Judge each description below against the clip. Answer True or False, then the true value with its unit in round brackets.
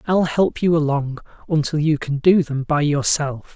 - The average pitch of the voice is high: False (150 Hz)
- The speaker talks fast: False (185 wpm)